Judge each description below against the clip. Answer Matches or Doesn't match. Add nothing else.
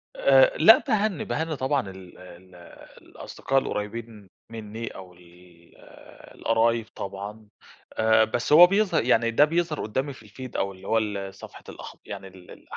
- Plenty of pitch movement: Matches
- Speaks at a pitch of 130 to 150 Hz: Doesn't match